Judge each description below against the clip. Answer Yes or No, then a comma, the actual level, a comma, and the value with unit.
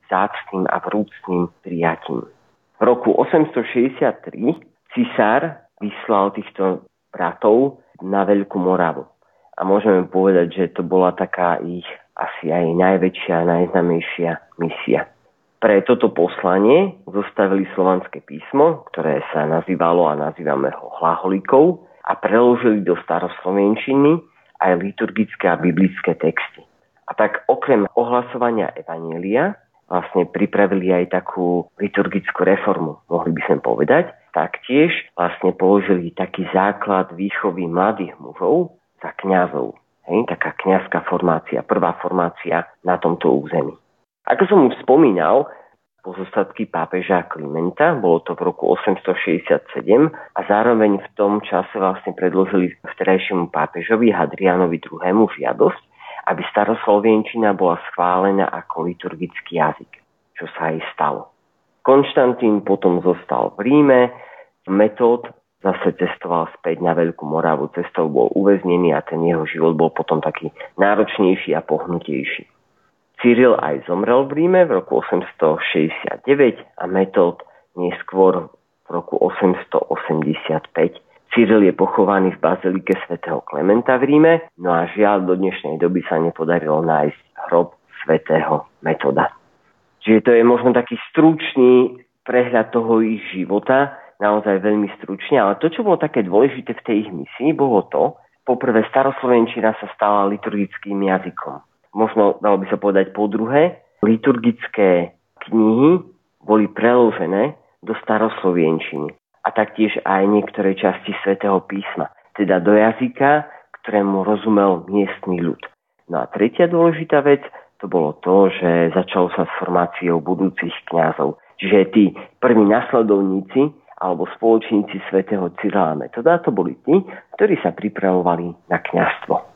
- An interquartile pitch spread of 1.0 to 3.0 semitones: No, average, 3.8 semitones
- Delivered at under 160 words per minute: Yes, average, 125 wpm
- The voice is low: Yes, low, 100 Hz